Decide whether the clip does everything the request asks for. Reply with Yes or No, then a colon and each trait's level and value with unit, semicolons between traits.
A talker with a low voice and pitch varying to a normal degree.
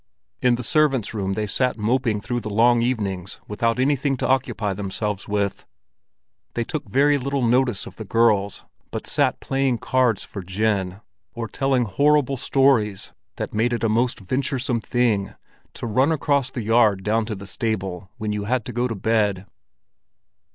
Yes: low, 115 Hz; average, 3.7 semitones